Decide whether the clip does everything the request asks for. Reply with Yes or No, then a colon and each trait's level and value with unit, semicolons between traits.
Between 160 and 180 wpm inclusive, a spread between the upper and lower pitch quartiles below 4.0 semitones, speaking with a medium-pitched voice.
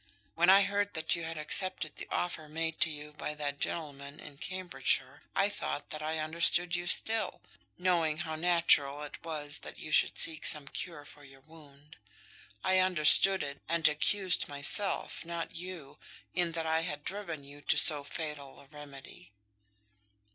Yes: average, 170 wpm; average, 2.9 semitones; medium, 160 Hz